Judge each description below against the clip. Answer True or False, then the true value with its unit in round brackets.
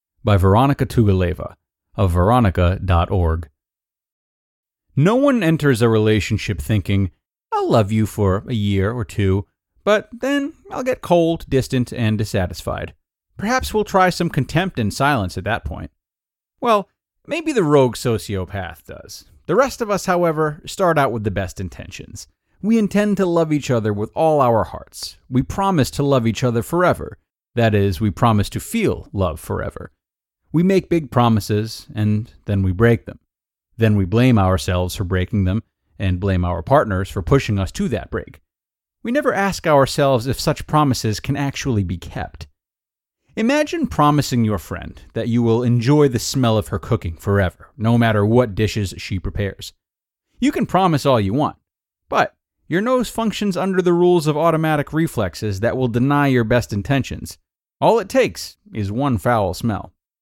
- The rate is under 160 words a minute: False (165 wpm)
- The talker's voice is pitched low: True (115 Hz)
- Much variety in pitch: True (7.3 semitones)